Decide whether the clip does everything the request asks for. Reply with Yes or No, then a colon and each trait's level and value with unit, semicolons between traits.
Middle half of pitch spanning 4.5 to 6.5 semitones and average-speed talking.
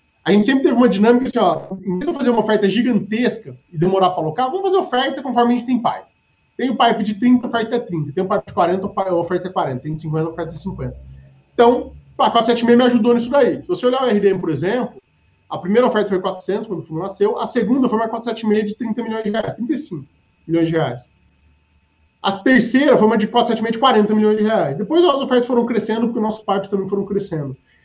No: average, 5.0 semitones; fast, 240 wpm